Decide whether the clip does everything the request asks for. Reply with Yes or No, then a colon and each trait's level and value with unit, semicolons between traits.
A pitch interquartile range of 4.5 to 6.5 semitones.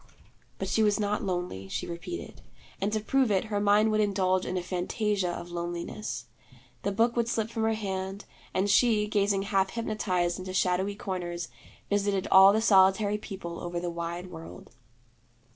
No: average, 2.8 semitones